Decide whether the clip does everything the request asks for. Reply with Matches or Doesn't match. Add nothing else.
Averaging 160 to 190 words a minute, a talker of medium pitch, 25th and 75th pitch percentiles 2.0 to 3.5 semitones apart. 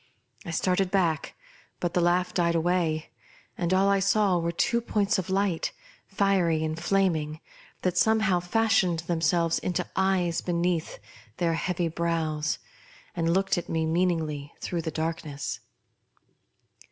Doesn't match